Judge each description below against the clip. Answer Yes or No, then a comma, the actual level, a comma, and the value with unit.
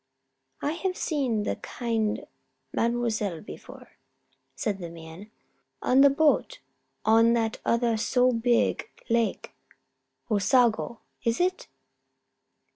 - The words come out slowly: Yes, slow, 105 wpm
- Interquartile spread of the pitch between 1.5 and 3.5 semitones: Yes, average, 2.8 semitones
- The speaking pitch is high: Yes, high, 235 Hz